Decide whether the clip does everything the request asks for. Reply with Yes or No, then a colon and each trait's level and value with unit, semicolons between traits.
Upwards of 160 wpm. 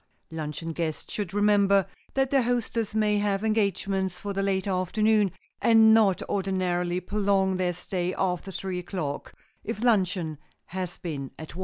No: average, 145 wpm